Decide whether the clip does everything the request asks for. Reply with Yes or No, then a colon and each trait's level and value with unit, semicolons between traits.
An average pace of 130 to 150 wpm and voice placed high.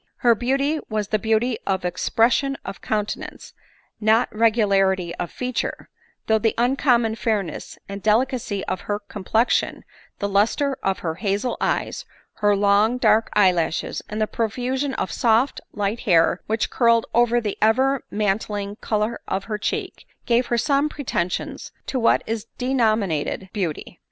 Yes: average, 145 wpm; high, 220 Hz